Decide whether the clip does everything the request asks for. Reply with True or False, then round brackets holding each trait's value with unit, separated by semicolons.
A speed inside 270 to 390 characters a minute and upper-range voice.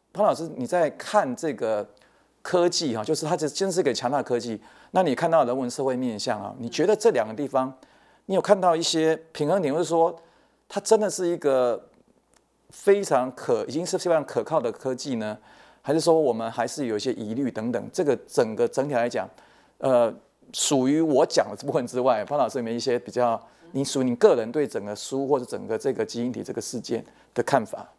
False (305 characters per minute; 140 Hz)